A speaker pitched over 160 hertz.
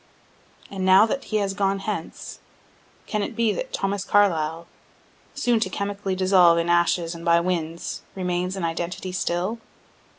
Yes: medium, 185 Hz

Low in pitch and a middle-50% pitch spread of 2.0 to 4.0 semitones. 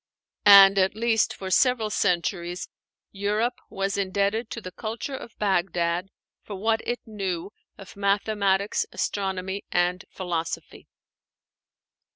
No: high, 195 Hz; narrow, 2.4 semitones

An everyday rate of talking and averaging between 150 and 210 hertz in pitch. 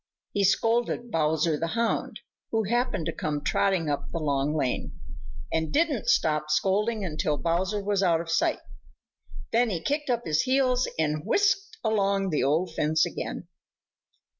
Yes: average, 155 wpm; medium, 185 Hz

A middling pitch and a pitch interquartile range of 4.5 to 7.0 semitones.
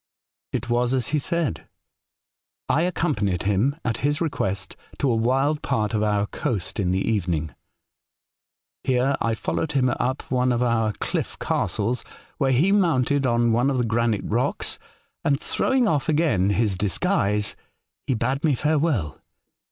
No: low, 125 Hz; average, 5.2 semitones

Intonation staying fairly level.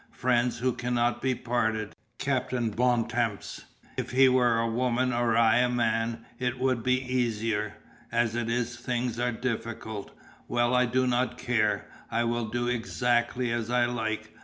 Yes: narrow, 1.5 semitones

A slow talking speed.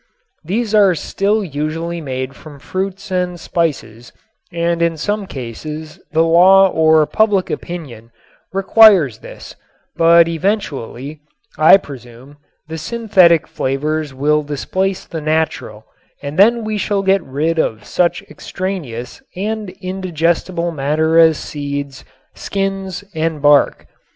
Yes: slow, 120 wpm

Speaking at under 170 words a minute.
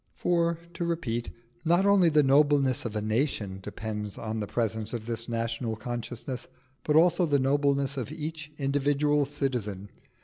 Yes: average, 150 wpm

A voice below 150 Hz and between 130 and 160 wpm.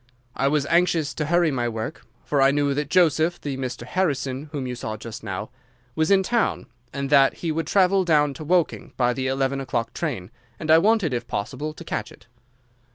No: medium, 140 Hz; average, 195 wpm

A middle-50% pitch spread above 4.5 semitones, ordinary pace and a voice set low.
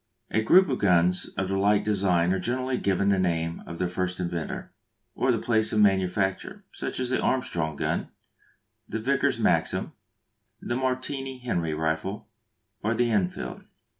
Yes: average, 5.3 semitones; average, 160 wpm; low, 100 Hz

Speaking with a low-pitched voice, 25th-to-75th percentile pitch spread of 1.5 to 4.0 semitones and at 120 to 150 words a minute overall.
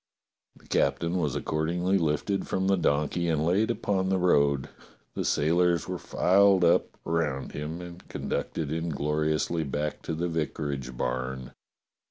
Yes: very low, 80 Hz; average, 3.2 semitones; average, 140 wpm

